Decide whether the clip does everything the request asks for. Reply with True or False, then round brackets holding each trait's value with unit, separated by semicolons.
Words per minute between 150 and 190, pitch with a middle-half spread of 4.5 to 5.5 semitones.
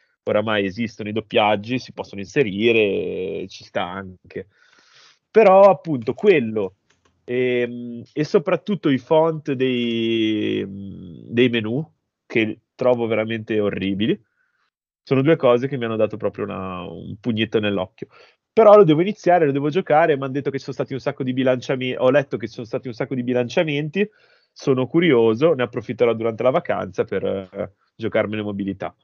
True (155 wpm; 5.0 semitones)